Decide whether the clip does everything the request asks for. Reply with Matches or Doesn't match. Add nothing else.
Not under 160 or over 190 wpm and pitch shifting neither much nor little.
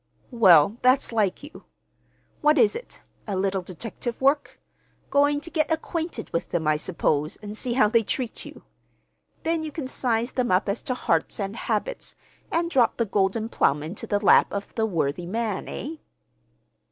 Doesn't match